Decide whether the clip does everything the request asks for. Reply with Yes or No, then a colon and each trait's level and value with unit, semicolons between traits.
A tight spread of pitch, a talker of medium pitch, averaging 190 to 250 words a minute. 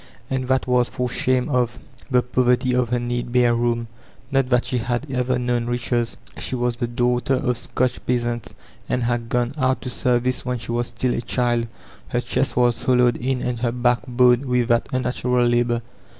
No: narrow, 0.9 semitones; low, 125 Hz; average, 195 wpm